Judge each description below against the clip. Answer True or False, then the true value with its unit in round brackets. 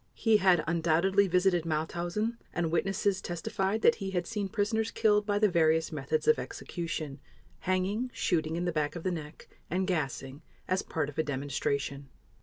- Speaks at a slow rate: False (170 wpm)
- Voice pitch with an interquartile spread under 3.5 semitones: False (4.1 semitones)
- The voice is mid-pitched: True (175 Hz)